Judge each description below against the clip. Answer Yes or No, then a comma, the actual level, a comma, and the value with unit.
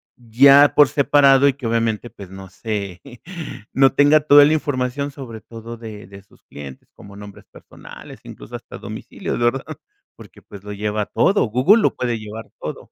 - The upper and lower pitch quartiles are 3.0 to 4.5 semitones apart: No, average, 5.2 semitones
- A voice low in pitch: Yes, low, 120 Hz